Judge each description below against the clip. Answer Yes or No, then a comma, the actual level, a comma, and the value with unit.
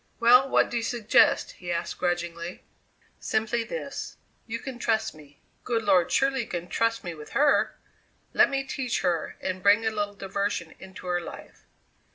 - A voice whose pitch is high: Yes, high, 205 Hz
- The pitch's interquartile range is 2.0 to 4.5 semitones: No, average, 5.0 semitones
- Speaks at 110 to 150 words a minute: No, average, 175 wpm